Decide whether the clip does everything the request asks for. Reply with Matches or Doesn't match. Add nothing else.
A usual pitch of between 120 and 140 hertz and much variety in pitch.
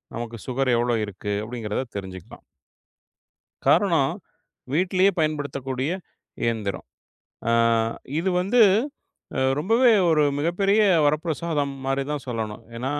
Matches